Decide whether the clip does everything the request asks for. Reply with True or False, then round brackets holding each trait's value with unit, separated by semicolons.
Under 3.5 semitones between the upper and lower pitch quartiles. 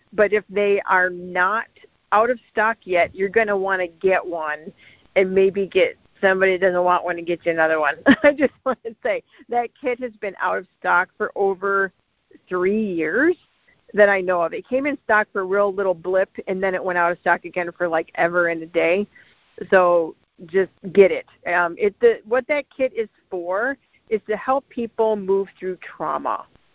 False (3.8 semitones)